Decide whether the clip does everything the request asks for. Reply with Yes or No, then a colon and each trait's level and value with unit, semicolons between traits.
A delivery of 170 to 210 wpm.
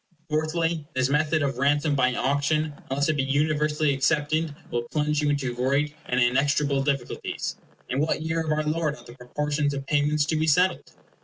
Yes: average, 180 wpm